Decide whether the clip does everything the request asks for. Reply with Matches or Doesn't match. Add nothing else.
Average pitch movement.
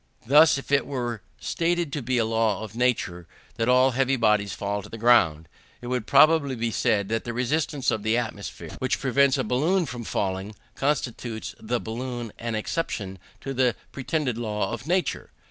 Matches